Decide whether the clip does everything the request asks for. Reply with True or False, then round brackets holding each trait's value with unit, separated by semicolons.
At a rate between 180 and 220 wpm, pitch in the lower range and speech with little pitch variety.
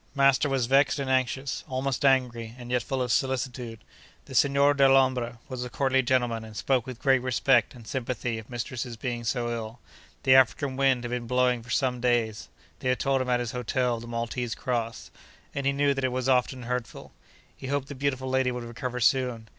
True (200 wpm; 125 Hz; 1.9 semitones)